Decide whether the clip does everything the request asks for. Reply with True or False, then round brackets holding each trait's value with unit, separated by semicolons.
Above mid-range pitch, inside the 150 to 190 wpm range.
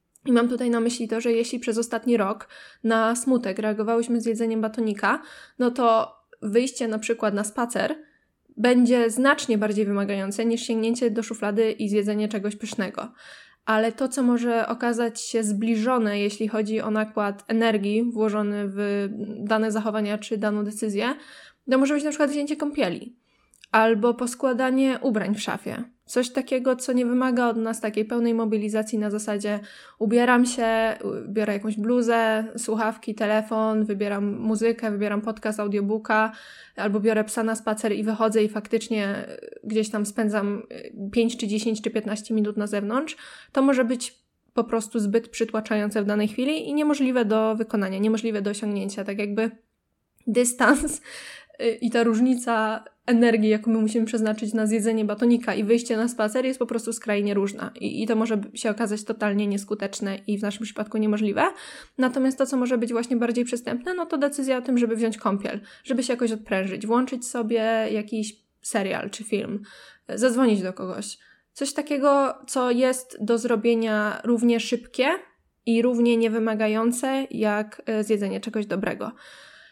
True (225 Hz; 155 wpm)